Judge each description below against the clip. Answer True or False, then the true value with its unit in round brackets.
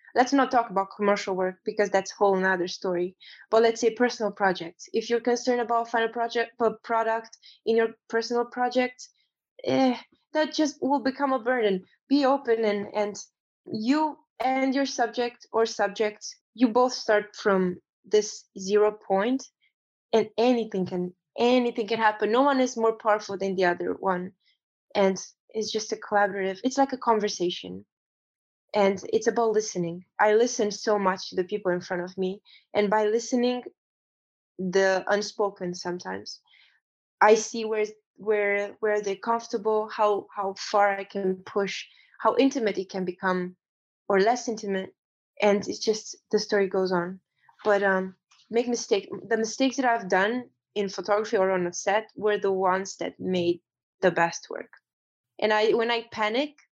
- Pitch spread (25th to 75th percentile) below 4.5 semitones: True (3.4 semitones)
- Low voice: False (215 Hz)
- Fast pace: False (165 wpm)